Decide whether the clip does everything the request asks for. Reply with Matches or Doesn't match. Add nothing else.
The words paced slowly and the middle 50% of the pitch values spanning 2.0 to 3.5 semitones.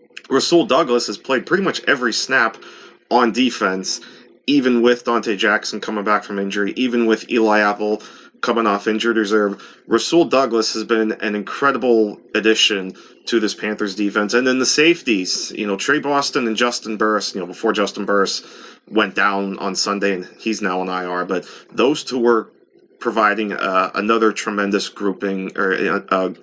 Doesn't match